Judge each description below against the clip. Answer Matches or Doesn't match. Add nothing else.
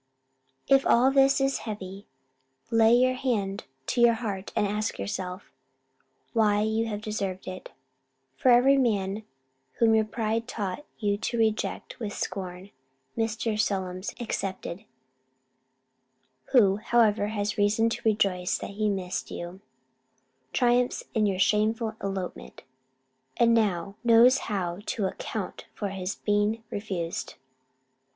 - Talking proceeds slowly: Matches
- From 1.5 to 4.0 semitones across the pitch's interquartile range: Matches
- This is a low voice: Doesn't match